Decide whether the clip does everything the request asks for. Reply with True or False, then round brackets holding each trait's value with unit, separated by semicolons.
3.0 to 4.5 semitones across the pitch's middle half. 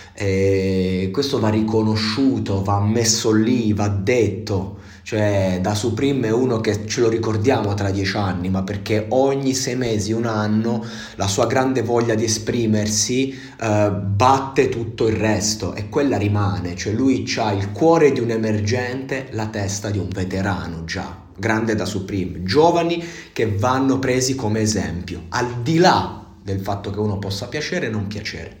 True (3.3 semitones)